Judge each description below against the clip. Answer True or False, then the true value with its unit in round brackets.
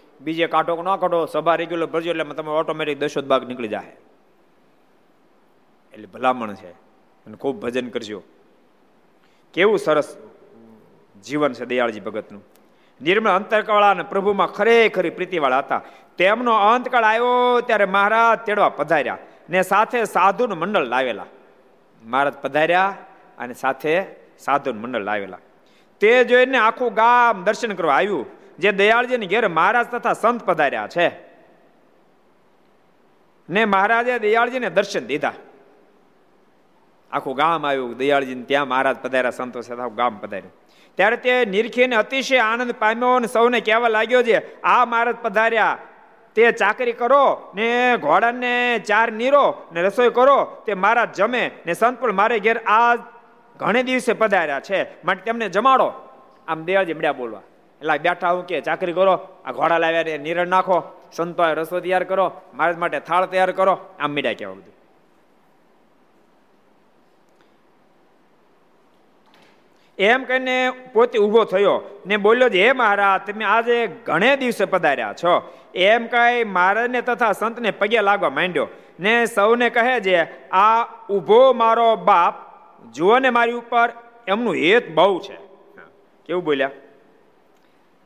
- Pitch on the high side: True (205 Hz)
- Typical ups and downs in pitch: False (6.0 semitones)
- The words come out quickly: False (120 wpm)